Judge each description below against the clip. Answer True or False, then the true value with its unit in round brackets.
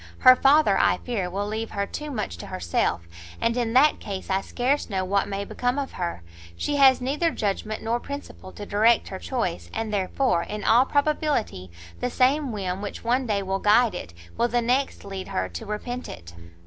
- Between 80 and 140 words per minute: False (200 wpm)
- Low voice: False (220 Hz)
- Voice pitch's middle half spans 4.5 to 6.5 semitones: True (4.8 semitones)